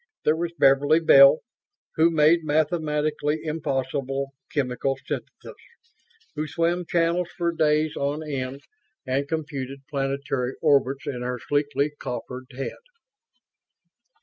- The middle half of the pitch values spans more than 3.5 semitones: No, narrow, 2.5 semitones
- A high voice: No, medium, 145 Hz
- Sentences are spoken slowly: Yes, slow, 110 wpm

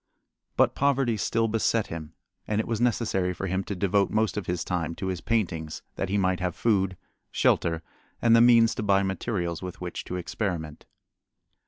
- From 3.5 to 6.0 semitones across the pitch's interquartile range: Yes, average, 4.0 semitones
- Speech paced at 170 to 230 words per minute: Yes, average, 185 wpm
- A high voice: No, very low, 95 Hz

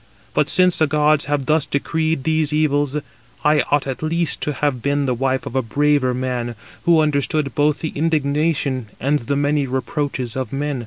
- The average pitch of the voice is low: No, medium, 145 Hz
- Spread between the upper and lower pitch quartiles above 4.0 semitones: No, narrow, 2.5 semitones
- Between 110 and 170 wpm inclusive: No, average, 180 wpm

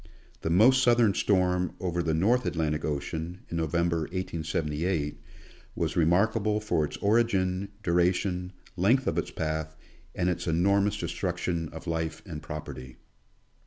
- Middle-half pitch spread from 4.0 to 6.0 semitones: No, average, 3.3 semitones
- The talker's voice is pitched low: Yes, very low, 85 Hz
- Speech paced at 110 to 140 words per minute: Yes, slow, 135 wpm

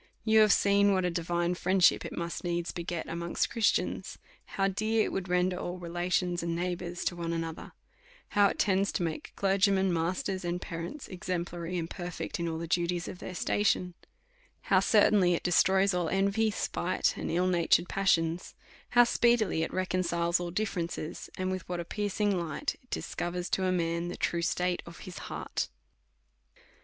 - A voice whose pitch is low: No, medium, 180 Hz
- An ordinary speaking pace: Yes, average, 175 wpm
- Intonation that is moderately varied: No, narrow, 2.2 semitones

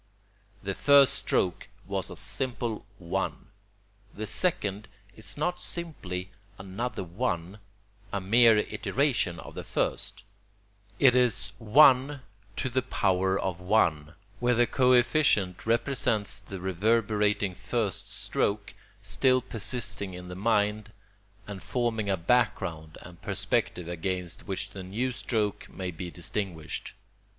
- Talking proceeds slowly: Yes, slow, 110 wpm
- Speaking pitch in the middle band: No, low, 105 Hz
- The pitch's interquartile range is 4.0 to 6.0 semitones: Yes, average, 4.7 semitones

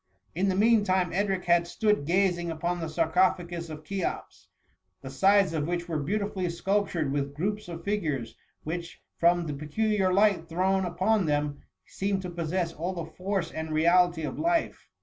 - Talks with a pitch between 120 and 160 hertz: No, medium, 175 Hz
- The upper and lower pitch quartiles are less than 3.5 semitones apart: Yes, average, 3.1 semitones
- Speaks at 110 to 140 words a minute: No, average, 170 wpm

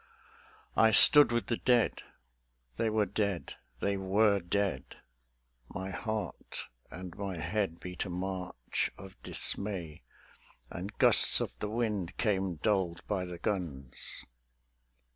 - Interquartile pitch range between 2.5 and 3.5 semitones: Yes, average, 3.0 semitones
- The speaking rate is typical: No, slow, 125 wpm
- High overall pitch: No, very low, 95 Hz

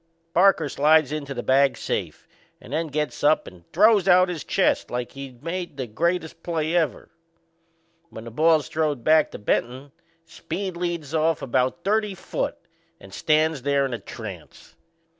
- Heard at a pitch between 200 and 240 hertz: No, medium, 155 Hz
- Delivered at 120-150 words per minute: No, average, 160 wpm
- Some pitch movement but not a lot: Yes, average, 4.1 semitones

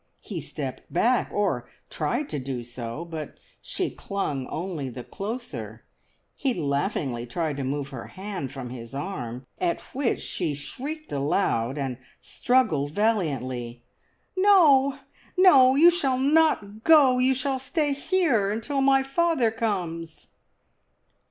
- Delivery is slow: Yes, slow, 130 wpm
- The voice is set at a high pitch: Yes, high, 195 Hz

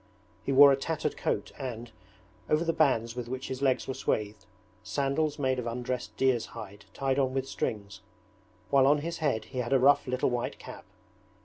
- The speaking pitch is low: Yes, low, 130 Hz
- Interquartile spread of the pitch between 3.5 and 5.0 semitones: No, average, 2.7 semitones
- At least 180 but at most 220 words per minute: Yes, average, 190 wpm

